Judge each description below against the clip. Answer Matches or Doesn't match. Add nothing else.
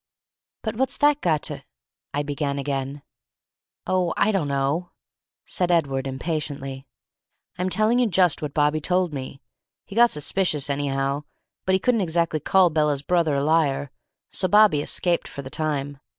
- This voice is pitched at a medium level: Matches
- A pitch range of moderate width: Matches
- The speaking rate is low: Doesn't match